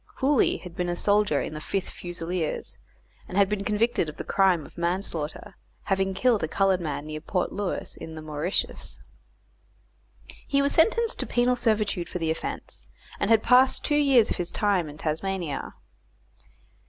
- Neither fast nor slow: Yes, average, 170 wpm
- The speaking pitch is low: No, high, 190 Hz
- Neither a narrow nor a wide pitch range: Yes, average, 4.7 semitones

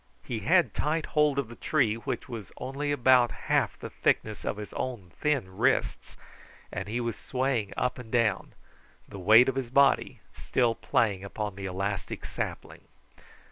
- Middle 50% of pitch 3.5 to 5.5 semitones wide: Yes, average, 4.3 semitones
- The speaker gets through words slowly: No, average, 165 wpm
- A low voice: Yes, low, 120 Hz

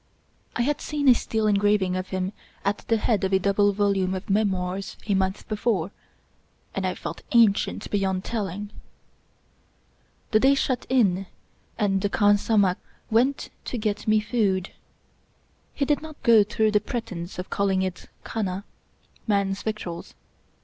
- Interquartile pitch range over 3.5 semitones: No, narrow, 2.6 semitones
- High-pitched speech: Yes, high, 205 Hz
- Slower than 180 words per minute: Yes, average, 160 wpm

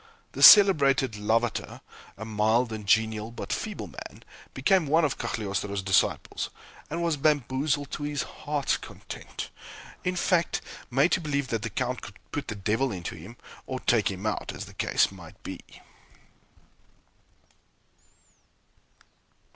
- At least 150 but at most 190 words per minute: No, average, 140 wpm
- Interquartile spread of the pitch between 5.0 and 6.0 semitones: Yes, average, 5.3 semitones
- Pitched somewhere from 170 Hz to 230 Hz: No, low, 125 Hz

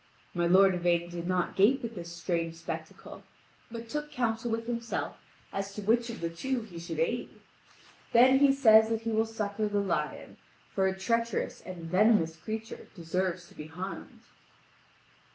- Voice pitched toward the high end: Yes, high, 205 Hz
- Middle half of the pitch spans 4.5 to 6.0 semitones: Yes, average, 4.8 semitones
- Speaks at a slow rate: No, average, 170 wpm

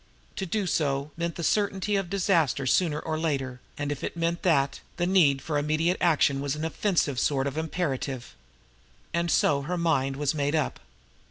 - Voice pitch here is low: No, medium, 155 Hz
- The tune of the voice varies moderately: Yes, average, 3.5 semitones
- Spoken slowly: No, average, 180 wpm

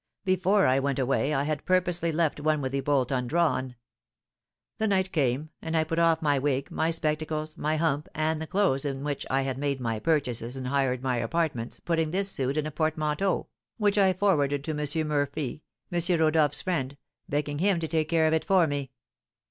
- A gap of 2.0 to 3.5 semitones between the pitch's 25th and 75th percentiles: Yes, average, 3.2 semitones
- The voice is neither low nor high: Yes, medium, 155 Hz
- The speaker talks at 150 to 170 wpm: No, average, 195 wpm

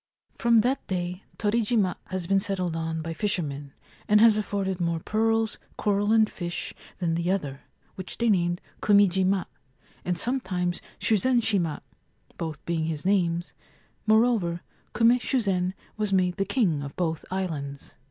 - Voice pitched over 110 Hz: Yes, medium, 185 Hz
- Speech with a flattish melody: No, average, 3.8 semitones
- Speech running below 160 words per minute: Yes, average, 145 wpm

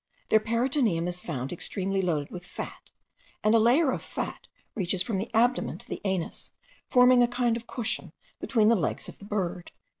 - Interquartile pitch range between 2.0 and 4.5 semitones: No, average, 4.9 semitones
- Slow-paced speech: No, average, 185 wpm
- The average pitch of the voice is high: Yes, high, 215 Hz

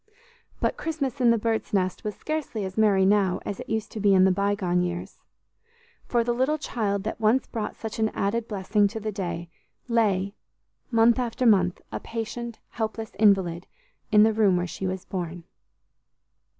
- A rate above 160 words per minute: Yes, average, 175 wpm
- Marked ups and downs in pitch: No, average, 3.1 semitones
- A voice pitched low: No, high, 210 Hz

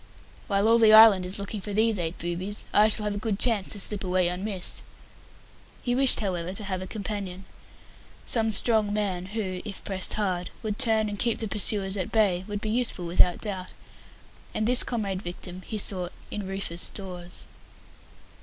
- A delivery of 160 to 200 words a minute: Yes, average, 180 wpm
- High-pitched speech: Yes, high, 200 Hz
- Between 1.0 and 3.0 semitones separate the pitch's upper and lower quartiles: Yes, average, 2.7 semitones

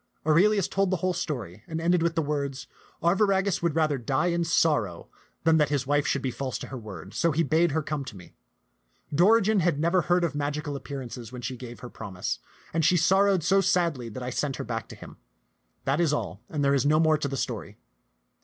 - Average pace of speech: No, fast, 220 wpm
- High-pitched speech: No, medium, 150 Hz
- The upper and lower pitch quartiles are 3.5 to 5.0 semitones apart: Yes, average, 4.6 semitones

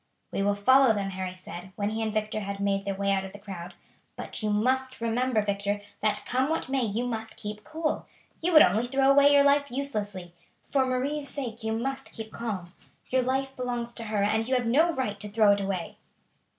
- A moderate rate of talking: No, fast, 215 wpm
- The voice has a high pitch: Yes, high, 225 Hz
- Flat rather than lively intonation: No, average, 4.5 semitones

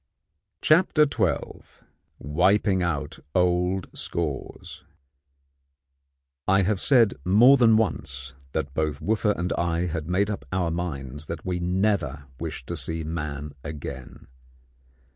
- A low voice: Yes, very low, 90 Hz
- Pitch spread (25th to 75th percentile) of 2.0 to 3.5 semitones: No, average, 4.7 semitones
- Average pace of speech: No, slow, 120 wpm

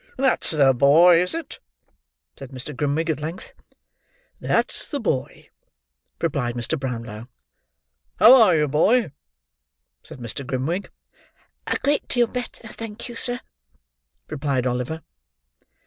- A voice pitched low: No, medium, 155 Hz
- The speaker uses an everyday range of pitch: No, wide, 8.8 semitones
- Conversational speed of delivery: No, slow, 120 wpm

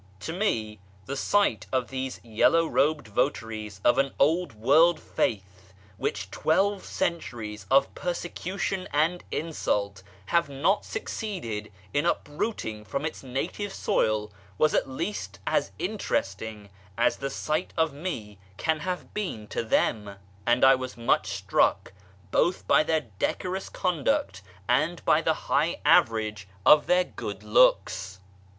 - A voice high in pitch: No, low, 135 Hz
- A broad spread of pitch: Yes, wide, 7.9 semitones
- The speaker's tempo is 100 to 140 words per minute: Yes, slow, 135 wpm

